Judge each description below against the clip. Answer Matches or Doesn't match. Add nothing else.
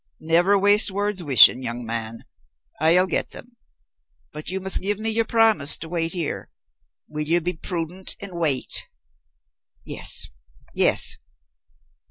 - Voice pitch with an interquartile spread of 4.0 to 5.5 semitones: Matches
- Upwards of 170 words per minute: Doesn't match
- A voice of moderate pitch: Matches